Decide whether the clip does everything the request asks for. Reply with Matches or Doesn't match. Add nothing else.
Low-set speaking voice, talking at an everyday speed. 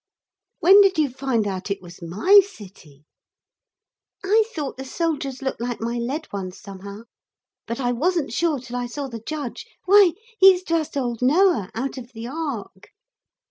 Doesn't match